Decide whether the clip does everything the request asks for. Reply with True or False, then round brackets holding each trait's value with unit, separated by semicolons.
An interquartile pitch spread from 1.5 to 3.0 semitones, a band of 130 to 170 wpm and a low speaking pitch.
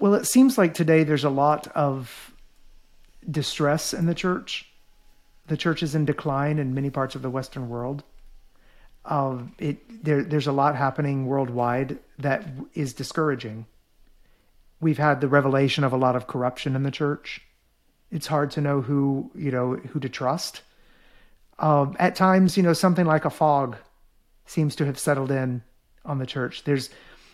False (2.5 semitones; 165 wpm; 145 Hz)